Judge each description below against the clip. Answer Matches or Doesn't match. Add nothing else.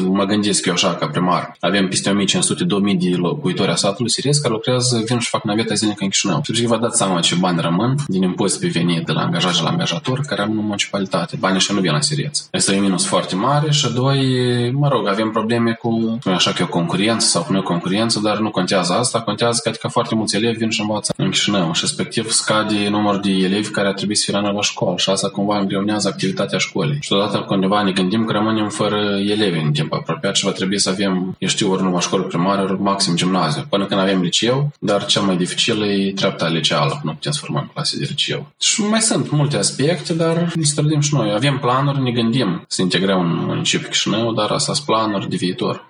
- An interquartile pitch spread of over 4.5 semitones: Doesn't match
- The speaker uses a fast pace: Matches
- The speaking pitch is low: Matches